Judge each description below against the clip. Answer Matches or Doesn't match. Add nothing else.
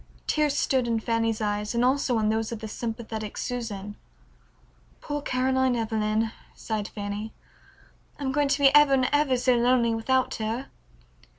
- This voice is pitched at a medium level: Doesn't match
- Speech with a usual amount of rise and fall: Matches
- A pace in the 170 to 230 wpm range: Doesn't match